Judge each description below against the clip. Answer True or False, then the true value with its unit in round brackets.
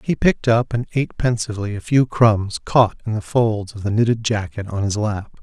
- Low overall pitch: True (110 Hz)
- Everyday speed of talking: False (220 wpm)